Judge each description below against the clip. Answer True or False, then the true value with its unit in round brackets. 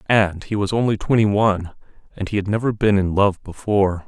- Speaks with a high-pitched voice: False (100 Hz)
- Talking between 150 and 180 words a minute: False (205 wpm)